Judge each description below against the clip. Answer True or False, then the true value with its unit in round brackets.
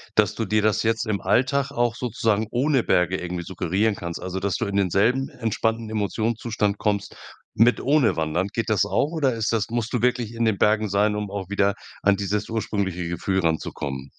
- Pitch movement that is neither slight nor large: True (3.0 semitones)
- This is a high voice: False (105 Hz)